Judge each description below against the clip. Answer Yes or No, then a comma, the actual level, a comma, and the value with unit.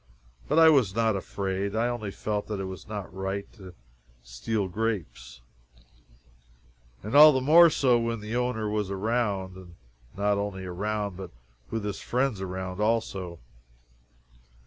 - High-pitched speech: No, low, 105 Hz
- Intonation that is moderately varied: Yes, average, 3.3 semitones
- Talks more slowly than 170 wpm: Yes, average, 145 wpm